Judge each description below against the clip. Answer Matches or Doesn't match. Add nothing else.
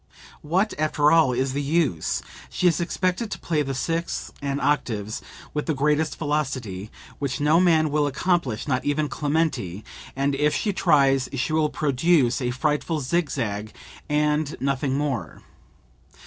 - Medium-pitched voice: Matches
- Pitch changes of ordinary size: Matches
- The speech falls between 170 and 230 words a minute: Doesn't match